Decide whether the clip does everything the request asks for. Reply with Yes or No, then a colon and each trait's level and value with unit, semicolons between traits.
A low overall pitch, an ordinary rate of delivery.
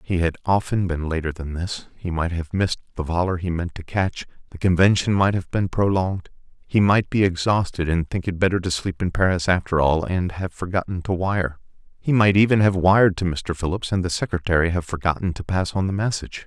No: very low, 90 Hz; fast, 220 wpm